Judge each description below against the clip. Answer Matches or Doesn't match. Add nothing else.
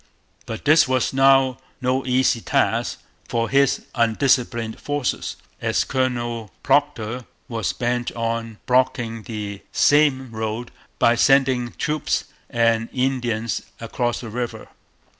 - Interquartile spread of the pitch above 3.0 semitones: Doesn't match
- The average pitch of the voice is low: Matches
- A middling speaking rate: Doesn't match